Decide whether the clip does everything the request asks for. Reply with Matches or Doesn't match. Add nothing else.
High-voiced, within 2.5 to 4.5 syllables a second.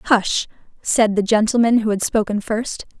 Matches